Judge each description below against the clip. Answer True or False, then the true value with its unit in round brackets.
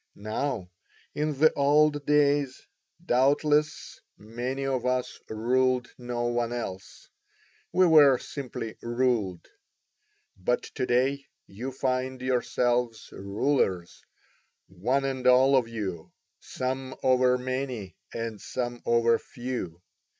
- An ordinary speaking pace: False (105 wpm)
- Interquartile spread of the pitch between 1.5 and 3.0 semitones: True (2.7 semitones)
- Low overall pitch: True (125 Hz)